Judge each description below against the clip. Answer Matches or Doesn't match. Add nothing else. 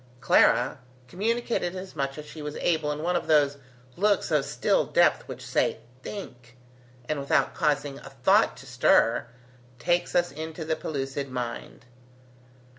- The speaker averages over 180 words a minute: Doesn't match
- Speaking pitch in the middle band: Matches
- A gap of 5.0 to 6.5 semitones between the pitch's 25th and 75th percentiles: Doesn't match